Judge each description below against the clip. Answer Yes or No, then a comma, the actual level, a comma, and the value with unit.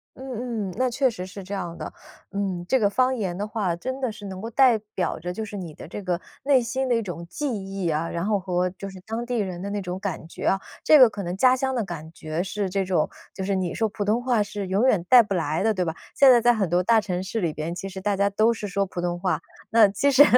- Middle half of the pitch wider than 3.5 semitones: Yes, average, 4.1 semitones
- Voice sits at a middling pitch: No, high, 200 Hz